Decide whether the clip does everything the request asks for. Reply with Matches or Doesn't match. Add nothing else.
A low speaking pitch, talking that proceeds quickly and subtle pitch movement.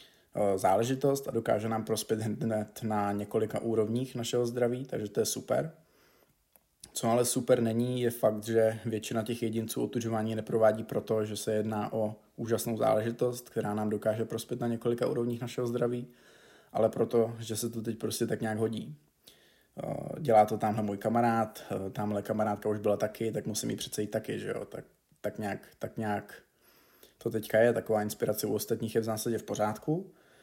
Matches